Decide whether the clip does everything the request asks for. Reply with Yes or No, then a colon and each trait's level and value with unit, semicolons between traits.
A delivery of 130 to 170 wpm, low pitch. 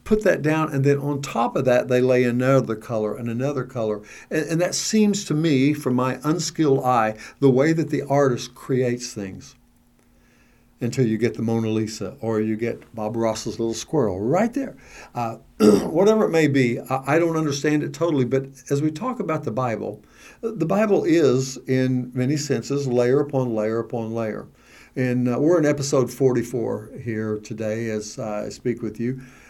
No: average, 185 wpm; low, 130 Hz